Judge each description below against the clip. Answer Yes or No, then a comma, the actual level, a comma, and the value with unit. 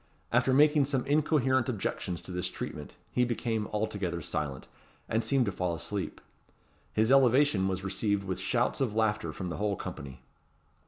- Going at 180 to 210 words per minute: No, average, 160 wpm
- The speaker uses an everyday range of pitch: No, wide, 5.7 semitones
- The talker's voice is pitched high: No, low, 105 Hz